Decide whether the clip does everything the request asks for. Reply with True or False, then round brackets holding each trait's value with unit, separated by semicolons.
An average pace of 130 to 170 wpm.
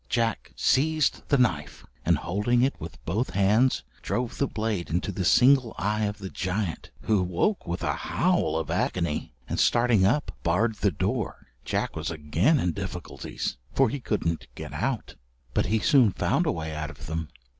False (180 wpm)